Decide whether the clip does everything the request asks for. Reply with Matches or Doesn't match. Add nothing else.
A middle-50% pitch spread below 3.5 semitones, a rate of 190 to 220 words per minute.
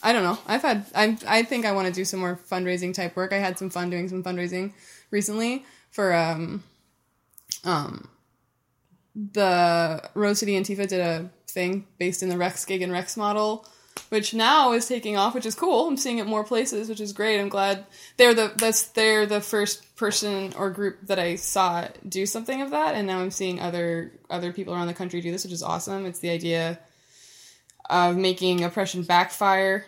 Matches